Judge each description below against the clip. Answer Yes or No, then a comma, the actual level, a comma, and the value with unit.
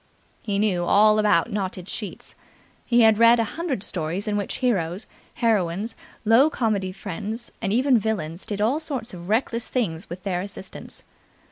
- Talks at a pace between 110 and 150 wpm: No, average, 160 wpm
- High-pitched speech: Yes, high, 210 Hz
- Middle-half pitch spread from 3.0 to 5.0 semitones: Yes, average, 3.7 semitones